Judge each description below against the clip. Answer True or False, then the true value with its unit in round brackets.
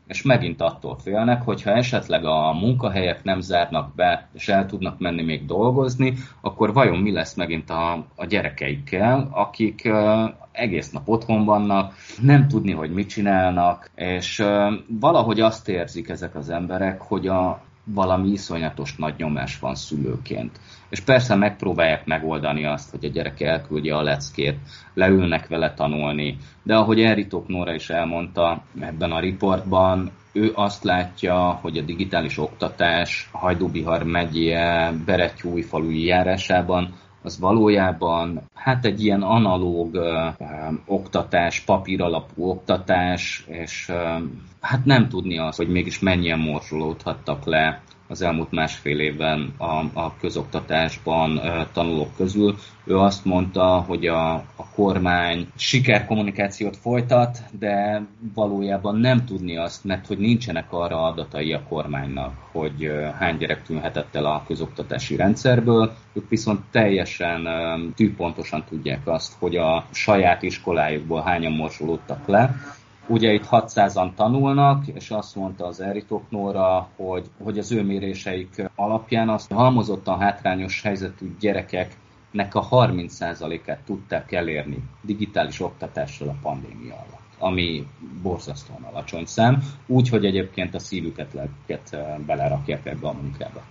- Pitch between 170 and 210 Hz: False (95 Hz)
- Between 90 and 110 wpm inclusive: False (125 wpm)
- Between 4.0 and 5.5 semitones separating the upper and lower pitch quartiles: True (4.3 semitones)